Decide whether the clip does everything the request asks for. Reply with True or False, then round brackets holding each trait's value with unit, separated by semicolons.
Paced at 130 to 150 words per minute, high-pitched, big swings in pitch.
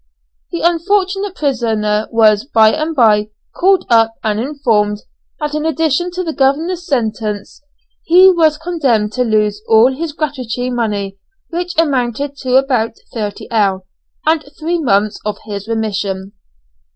True (135 wpm; 250 Hz; 6.9 semitones)